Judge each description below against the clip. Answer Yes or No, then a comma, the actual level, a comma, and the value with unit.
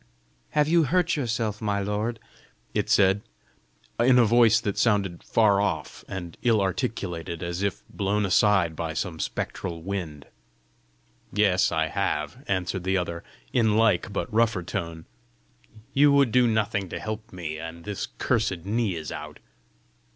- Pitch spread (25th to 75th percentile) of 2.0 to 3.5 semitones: No, average, 4.5 semitones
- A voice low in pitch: Yes, low, 100 Hz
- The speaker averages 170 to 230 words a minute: No, average, 150 wpm